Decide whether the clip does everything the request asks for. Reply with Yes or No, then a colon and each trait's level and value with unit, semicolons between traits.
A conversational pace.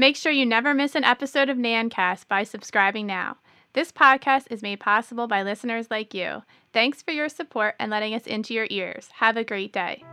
No: fast, 210 wpm